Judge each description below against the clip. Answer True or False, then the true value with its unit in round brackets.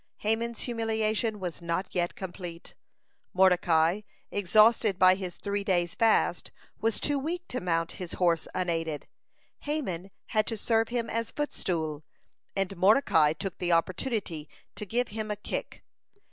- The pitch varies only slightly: False (4.4 semitones)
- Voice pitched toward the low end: False (195 Hz)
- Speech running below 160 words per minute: True (140 wpm)